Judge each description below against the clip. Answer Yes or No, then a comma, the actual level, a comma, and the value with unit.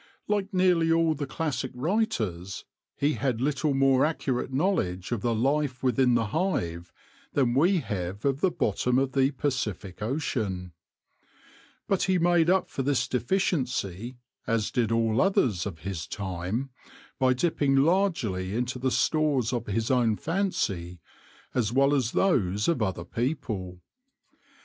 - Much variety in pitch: Yes, wide, 6.4 semitones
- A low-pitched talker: Yes, low, 130 Hz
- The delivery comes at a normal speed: Yes, average, 145 wpm